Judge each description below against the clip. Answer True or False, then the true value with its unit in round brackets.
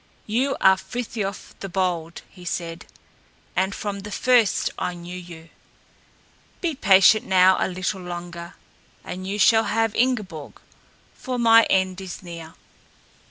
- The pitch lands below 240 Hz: True (190 Hz)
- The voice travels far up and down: False (3.6 semitones)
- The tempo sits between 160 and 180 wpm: False (135 wpm)